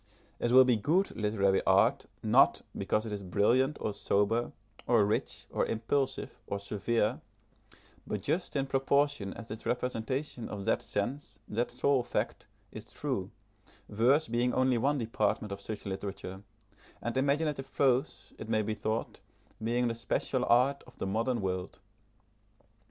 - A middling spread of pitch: Yes, average, 4.0 semitones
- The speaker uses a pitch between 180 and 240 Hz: No, low, 115 Hz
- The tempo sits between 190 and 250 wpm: No, average, 150 wpm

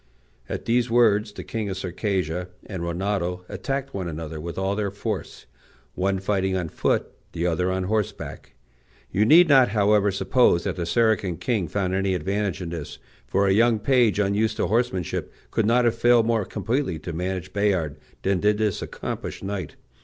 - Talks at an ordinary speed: Yes, average, 175 wpm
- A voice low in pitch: Yes, low, 100 Hz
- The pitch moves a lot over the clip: No, average, 3.3 semitones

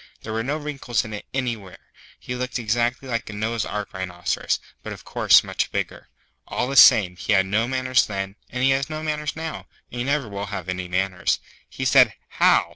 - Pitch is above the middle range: No, low, 115 Hz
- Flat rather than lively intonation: No, average, 4.7 semitones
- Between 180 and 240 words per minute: Yes, fast, 205 wpm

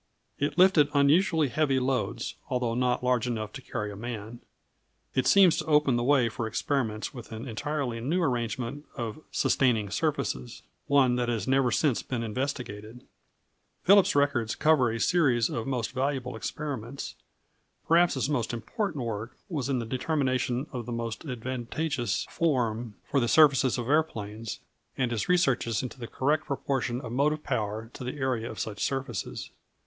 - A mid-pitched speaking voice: No, low, 125 Hz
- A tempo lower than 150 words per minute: No, average, 160 wpm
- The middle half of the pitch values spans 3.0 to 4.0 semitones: Yes, average, 3.7 semitones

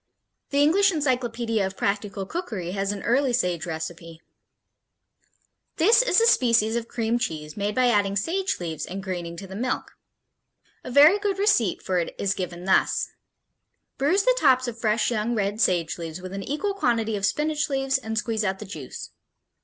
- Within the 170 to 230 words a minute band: Yes, average, 175 wpm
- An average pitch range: No, wide, 6.1 semitones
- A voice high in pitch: Yes, high, 220 Hz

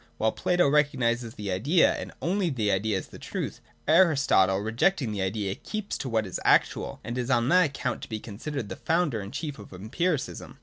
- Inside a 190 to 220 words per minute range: Yes, average, 200 wpm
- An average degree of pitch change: No, wide, 6.5 semitones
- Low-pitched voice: Yes, low, 120 Hz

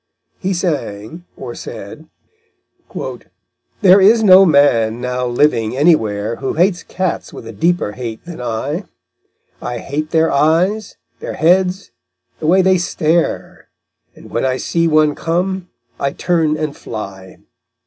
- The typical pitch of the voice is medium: Yes, medium, 155 Hz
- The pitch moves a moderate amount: No, wide, 6.4 semitones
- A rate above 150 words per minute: No, slow, 135 wpm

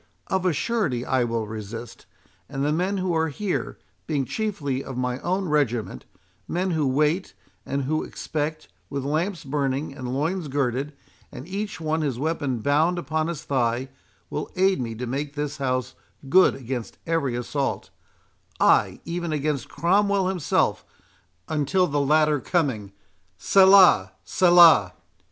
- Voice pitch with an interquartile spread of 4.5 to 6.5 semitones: Yes, average, 4.8 semitones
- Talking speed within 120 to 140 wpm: Yes, slow, 135 wpm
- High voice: No, medium, 150 Hz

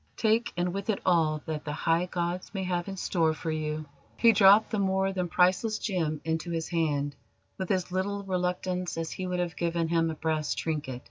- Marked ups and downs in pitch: No, average, 2.9 semitones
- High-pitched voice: No, medium, 175 Hz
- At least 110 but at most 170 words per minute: No, fast, 205 wpm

